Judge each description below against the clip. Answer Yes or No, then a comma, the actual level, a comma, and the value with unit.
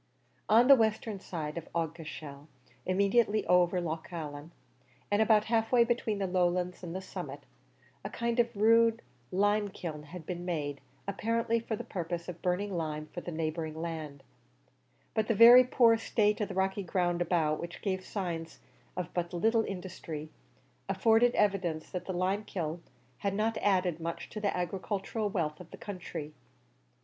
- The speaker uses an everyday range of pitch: Yes, average, 4.2 semitones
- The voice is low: No, medium, 185 Hz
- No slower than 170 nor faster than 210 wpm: No, average, 160 wpm